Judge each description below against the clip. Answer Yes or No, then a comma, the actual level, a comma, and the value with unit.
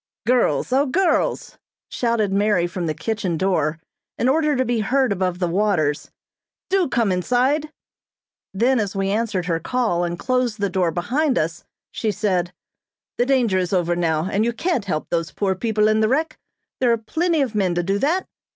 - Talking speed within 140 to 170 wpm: No, average, 185 wpm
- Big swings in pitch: Yes, wide, 5.8 semitones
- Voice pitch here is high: Yes, high, 210 Hz